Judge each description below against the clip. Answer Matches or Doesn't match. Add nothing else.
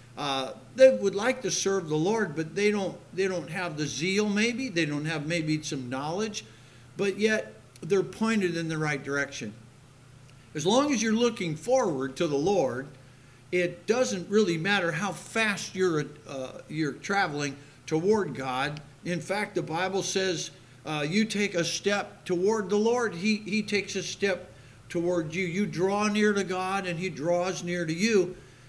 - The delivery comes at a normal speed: Matches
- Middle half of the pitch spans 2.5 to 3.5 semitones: Doesn't match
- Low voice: Doesn't match